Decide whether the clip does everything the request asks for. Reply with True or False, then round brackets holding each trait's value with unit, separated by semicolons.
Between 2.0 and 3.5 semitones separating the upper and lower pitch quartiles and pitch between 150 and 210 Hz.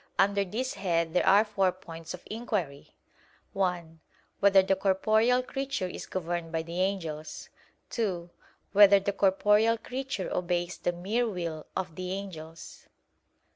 True (3.2 semitones; 190 Hz)